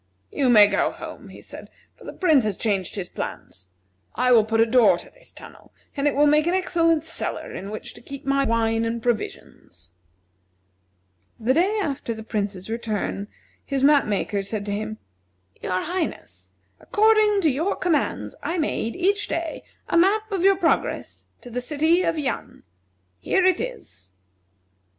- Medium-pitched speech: No, very high, 275 Hz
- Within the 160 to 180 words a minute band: Yes, average, 170 wpm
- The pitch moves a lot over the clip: Yes, wide, 7.9 semitones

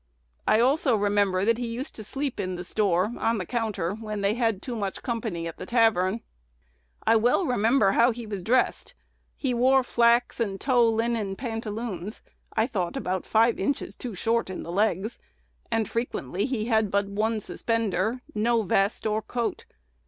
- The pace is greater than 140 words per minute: Yes, average, 175 wpm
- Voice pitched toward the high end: Yes, high, 220 Hz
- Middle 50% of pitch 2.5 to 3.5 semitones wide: Yes, average, 3.0 semitones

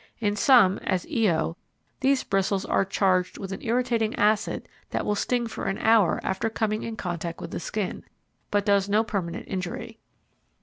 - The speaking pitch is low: No, high, 205 Hz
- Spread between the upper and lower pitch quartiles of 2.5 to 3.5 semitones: Yes, average, 3.0 semitones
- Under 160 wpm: No, average, 170 wpm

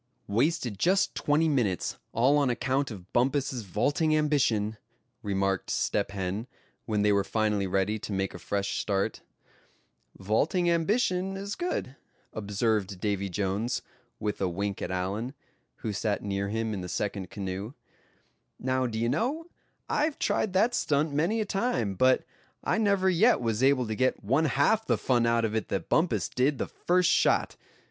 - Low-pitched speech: Yes, low, 115 Hz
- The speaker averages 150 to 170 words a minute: Yes, average, 160 wpm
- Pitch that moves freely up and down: Yes, wide, 7.2 semitones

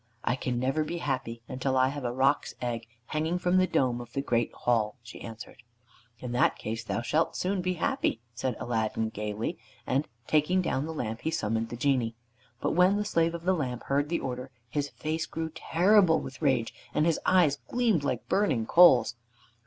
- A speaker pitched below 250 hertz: Yes, low, 135 Hz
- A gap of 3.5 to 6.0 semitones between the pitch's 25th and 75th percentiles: Yes, wide, 5.5 semitones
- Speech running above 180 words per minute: Yes, average, 195 wpm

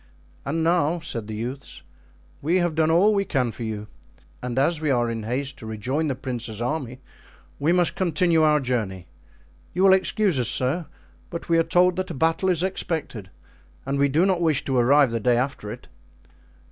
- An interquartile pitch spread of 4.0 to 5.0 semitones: No, wide, 5.6 semitones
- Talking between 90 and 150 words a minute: No, average, 195 wpm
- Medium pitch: Yes, medium, 145 Hz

